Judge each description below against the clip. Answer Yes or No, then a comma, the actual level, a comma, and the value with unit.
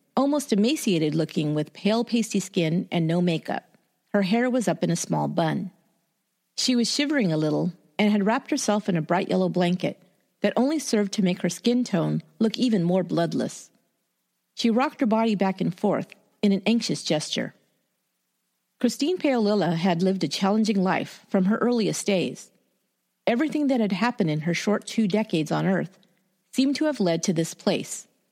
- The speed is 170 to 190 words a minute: Yes, average, 180 wpm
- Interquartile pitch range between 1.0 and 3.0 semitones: No, average, 4.6 semitones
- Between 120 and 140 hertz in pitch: No, high, 205 Hz